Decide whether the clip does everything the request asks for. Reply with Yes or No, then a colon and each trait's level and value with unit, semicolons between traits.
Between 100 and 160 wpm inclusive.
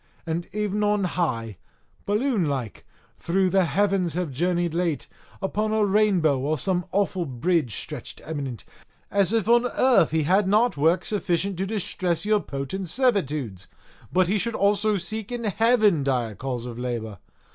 Yes: average, 155 wpm